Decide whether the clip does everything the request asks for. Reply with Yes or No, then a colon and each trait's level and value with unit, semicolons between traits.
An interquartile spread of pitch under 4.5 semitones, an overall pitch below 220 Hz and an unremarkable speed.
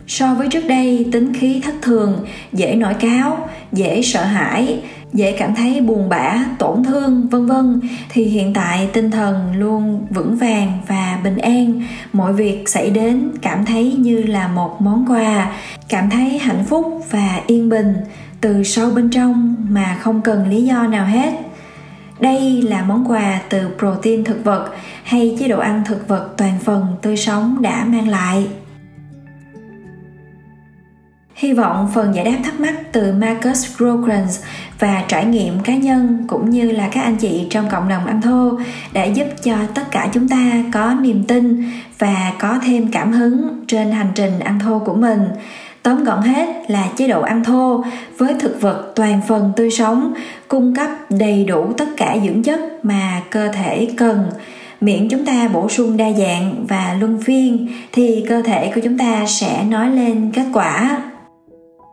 No: average, 3.4 semitones; high, 225 Hz; average, 175 wpm